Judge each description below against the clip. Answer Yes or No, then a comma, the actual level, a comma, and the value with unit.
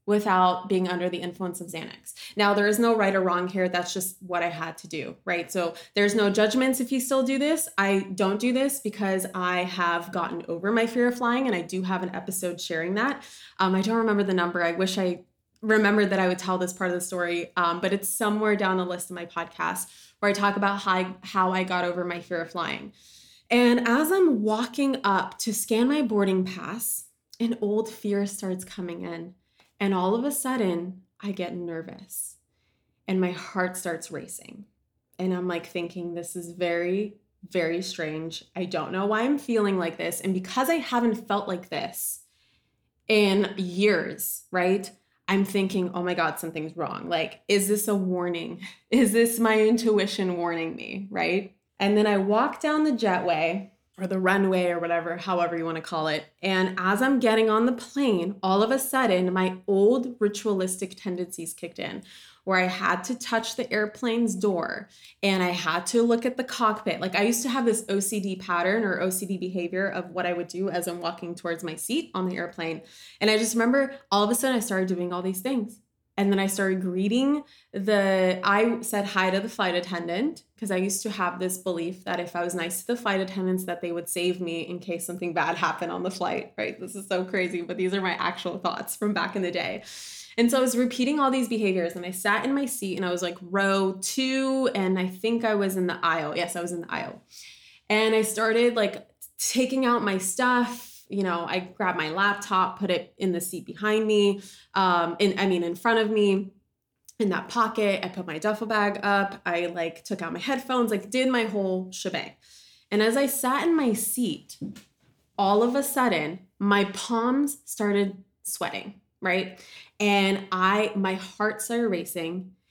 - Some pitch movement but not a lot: Yes, average, 3.4 semitones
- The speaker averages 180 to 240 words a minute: Yes, fast, 205 wpm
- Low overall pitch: No, high, 195 Hz